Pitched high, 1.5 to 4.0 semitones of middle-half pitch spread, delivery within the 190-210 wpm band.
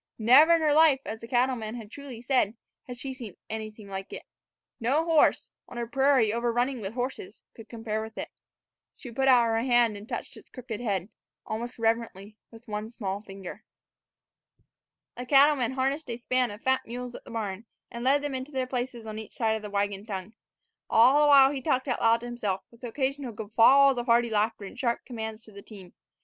Yes: high, 235 Hz; average, 3.2 semitones; average, 200 wpm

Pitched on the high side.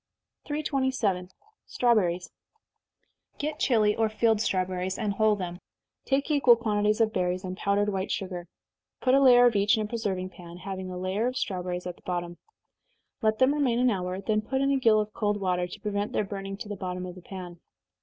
Yes: high, 205 Hz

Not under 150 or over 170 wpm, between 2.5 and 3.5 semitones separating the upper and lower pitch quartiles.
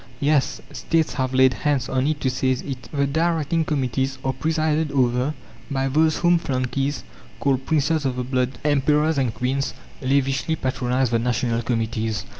Yes: average, 160 wpm; average, 2.8 semitones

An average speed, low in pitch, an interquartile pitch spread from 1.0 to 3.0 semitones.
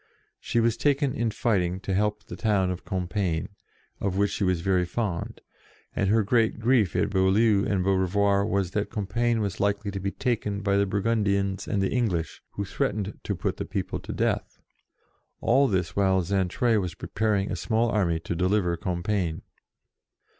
Yes: average, 170 wpm; low, 100 Hz; narrow, 2.4 semitones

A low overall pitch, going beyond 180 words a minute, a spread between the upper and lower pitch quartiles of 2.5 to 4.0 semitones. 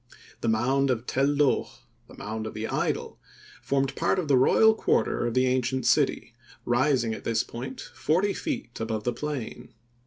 No: low, 130 Hz; average, 175 wpm; average, 3.4 semitones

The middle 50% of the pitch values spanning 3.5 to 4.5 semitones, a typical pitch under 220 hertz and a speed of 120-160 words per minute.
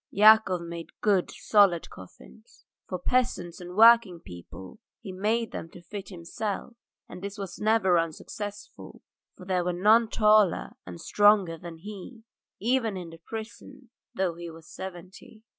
Yes: average, 3.9 semitones; high, 190 Hz; average, 145 wpm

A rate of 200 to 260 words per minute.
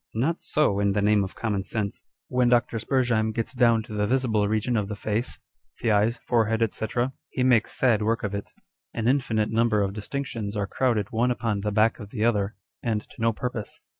Yes: fast, 205 wpm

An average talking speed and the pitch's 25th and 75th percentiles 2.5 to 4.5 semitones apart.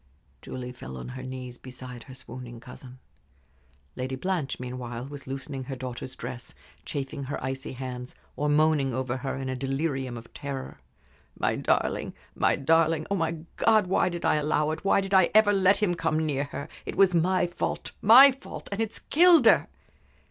No: average, 180 wpm; average, 5.1 semitones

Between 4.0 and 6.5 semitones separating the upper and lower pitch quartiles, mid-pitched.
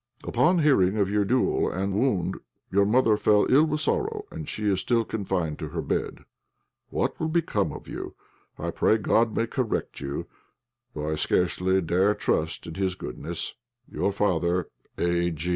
No: average, 5.1 semitones; low, 100 Hz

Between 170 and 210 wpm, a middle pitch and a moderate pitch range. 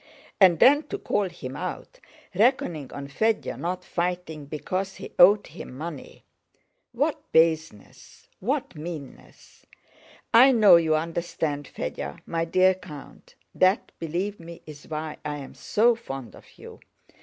No: slow, 135 wpm; medium, 170 Hz; average, 4.1 semitones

